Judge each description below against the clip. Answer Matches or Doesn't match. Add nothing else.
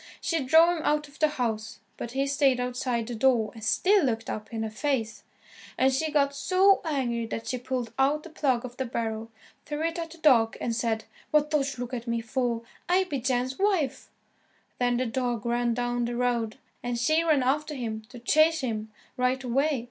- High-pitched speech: Matches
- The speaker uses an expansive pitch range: Doesn't match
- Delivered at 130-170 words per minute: Doesn't match